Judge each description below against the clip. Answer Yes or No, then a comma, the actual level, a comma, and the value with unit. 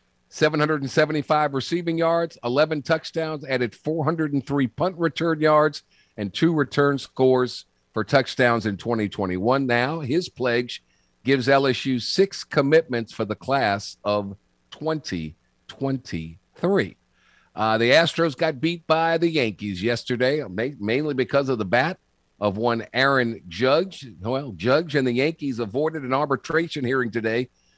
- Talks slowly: Yes, slow, 125 wpm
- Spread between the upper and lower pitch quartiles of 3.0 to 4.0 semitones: No, average, 4.9 semitones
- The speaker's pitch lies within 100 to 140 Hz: Yes, low, 135 Hz